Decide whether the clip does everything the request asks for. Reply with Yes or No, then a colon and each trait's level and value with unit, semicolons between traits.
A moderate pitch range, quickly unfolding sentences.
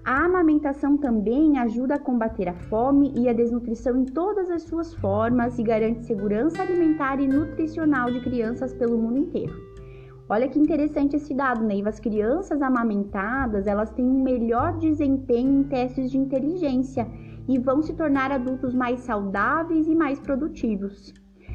No: average, 4.0 semitones; average, 155 wpm